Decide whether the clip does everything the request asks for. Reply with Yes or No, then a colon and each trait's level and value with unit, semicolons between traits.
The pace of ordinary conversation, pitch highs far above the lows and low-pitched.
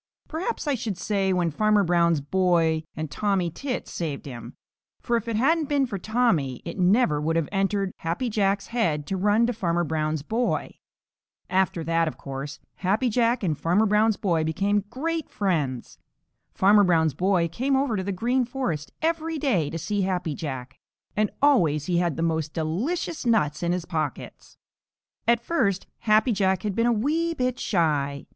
No: average, 175 wpm; wide, 6.1 semitones; high, 190 Hz